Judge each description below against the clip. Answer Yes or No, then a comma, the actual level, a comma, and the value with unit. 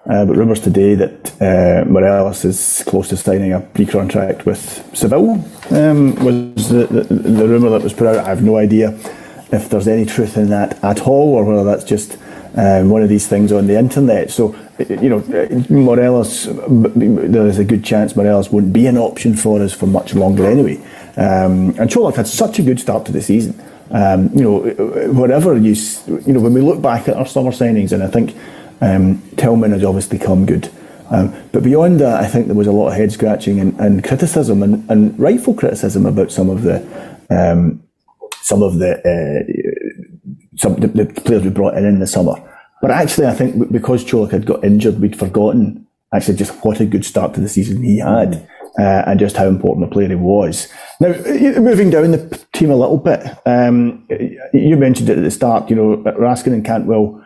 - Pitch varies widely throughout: No, average, 3.7 semitones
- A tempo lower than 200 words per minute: No, fast, 205 wpm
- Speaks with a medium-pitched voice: No, low, 110 Hz